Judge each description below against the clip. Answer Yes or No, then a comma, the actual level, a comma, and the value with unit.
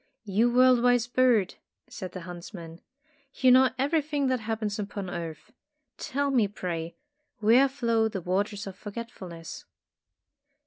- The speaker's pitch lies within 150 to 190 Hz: No, high, 220 Hz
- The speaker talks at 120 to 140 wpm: Yes, slow, 135 wpm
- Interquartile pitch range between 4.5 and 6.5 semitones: Yes, average, 5.2 semitones